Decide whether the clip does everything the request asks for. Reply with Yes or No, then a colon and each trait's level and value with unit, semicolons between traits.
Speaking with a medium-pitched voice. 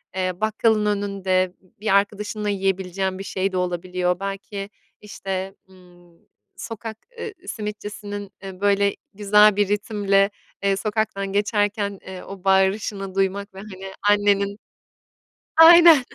No: high, 200 Hz